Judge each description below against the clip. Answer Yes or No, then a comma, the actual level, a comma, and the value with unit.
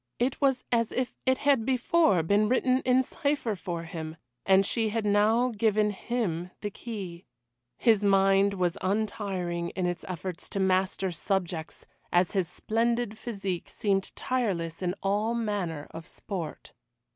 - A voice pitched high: Yes, high, 200 Hz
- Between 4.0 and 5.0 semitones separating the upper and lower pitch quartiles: Yes, average, 4.3 semitones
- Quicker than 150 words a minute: No, average, 145 wpm